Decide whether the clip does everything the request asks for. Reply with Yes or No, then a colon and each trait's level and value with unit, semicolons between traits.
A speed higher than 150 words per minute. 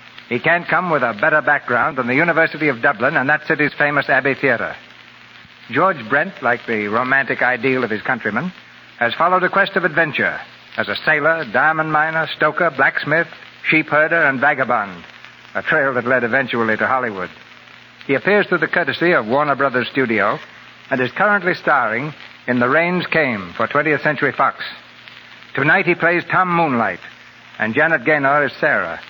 Yes: average, 165 wpm